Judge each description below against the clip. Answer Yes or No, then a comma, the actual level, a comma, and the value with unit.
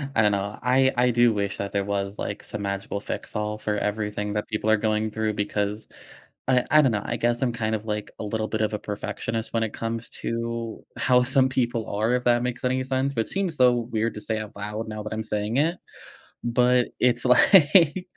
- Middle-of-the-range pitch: No, low, 110 Hz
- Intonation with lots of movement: No, average, 2.8 semitones